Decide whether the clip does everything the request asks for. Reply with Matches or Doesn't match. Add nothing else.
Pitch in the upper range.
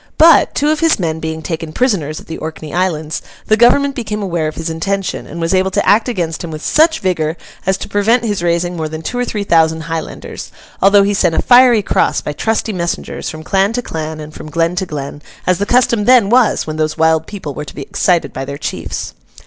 Doesn't match